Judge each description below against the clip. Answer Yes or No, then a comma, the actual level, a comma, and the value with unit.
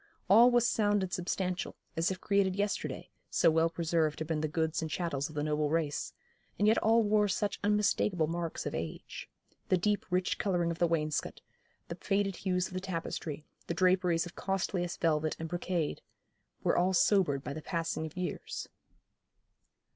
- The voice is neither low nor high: Yes, medium, 175 Hz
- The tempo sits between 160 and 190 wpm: Yes, average, 175 wpm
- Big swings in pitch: No, average, 3.3 semitones